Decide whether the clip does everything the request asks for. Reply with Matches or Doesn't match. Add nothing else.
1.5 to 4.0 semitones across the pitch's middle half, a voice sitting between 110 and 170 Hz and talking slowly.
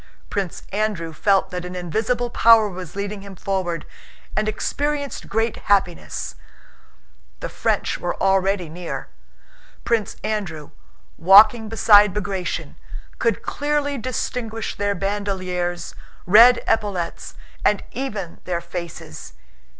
Doesn't match